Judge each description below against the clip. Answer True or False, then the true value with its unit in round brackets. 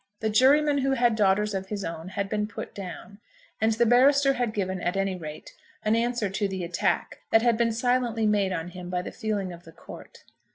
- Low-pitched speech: False (210 Hz)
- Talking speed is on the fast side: True (215 wpm)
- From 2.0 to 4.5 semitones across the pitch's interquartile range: True (4.0 semitones)